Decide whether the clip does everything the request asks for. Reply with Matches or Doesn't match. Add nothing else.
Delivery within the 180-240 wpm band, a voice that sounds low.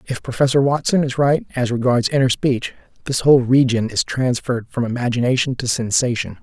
Doesn't match